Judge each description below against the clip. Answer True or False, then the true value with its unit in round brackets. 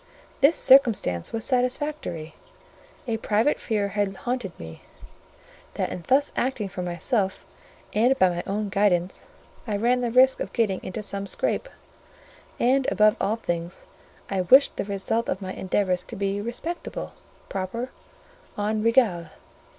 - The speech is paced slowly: False (145 wpm)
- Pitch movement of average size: True (4.7 semitones)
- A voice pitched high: True (210 Hz)